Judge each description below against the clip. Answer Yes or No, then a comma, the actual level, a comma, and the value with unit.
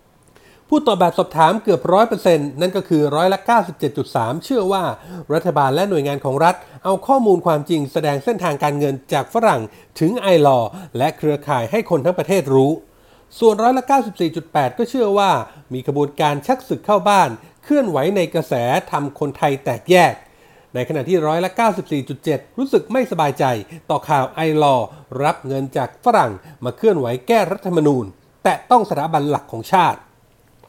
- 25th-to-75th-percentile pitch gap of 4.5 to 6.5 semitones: Yes, average, 5.3 semitones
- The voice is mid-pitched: Yes, medium, 160 Hz